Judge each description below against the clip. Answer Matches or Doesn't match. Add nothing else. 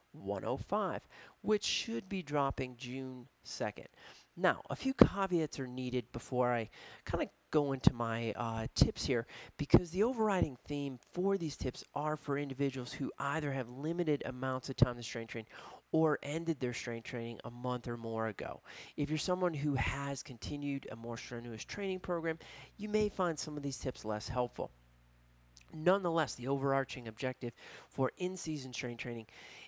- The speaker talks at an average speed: Matches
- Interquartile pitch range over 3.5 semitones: Matches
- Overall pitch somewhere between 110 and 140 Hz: Matches